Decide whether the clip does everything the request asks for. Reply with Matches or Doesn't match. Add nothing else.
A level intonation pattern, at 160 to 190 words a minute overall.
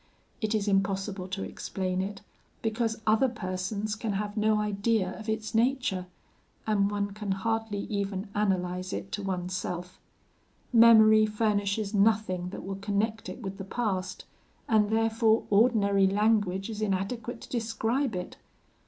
Doesn't match